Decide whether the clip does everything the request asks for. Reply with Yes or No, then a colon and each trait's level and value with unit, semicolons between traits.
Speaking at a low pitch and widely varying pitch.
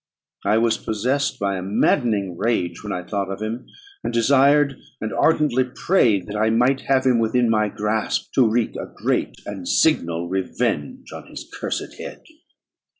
No: low, 110 Hz; average, 4.2 semitones